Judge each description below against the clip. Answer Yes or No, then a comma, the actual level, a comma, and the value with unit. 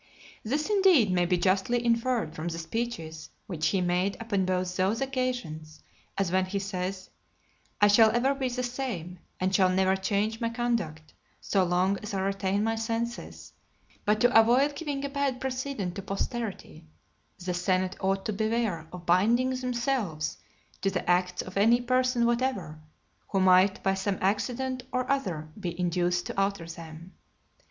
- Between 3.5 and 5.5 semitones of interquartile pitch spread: Yes, average, 4.9 semitones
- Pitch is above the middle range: Yes, high, 195 Hz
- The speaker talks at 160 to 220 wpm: Yes, average, 165 wpm